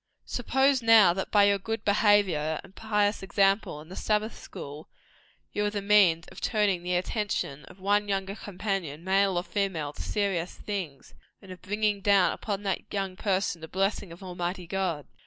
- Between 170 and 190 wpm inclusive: Yes, average, 175 wpm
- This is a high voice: Yes, high, 195 Hz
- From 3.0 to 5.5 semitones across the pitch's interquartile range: No, narrow, 2.6 semitones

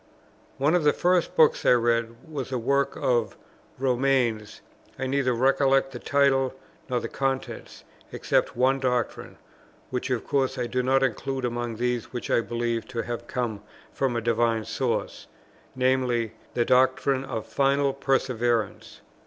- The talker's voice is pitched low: Yes, low, 125 Hz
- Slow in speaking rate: No, average, 150 wpm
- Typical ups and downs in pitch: No, narrow, 2.2 semitones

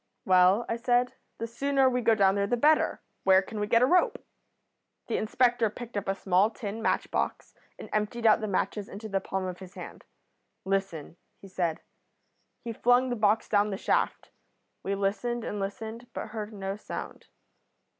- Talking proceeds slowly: No, average, 185 wpm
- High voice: Yes, high, 215 Hz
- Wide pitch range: No, average, 3.4 semitones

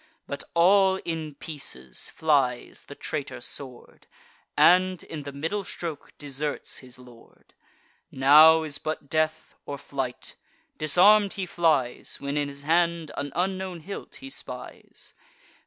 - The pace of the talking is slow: Yes, slow, 130 wpm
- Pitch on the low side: No, medium, 155 Hz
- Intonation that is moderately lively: Yes, average, 3.7 semitones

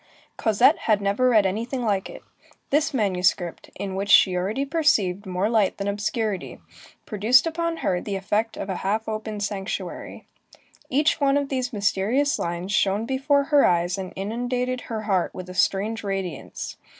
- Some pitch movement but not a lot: Yes, average, 4.7 semitones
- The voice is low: No, high, 210 Hz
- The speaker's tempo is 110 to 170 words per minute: Yes, average, 160 wpm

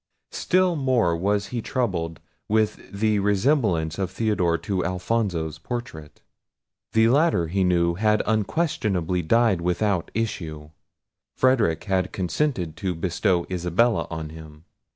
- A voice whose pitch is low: Yes, very low, 95 Hz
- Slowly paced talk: Yes, slow, 120 wpm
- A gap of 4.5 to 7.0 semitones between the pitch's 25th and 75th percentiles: Yes, average, 4.8 semitones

